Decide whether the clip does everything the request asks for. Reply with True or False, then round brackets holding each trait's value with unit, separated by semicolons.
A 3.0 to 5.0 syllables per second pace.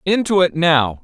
True (4.4 syllables/s)